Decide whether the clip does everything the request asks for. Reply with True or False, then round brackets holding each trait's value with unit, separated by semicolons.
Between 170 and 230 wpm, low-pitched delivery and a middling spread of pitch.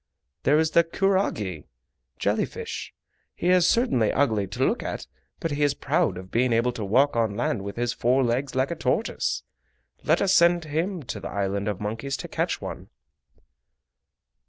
False (180 wpm; 130 Hz; 7.6 semitones)